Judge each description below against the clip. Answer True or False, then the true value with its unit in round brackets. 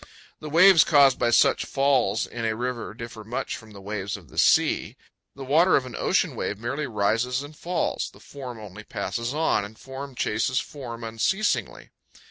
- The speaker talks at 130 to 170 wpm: False (180 wpm)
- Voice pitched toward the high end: False (120 Hz)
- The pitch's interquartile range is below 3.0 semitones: False (4.2 semitones)